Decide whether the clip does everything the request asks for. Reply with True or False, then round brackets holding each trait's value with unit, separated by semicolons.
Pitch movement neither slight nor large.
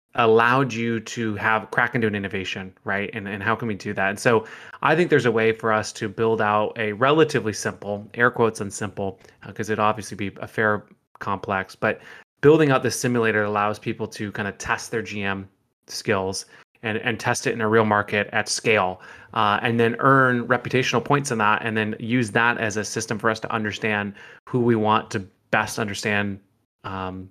False (2.2 semitones)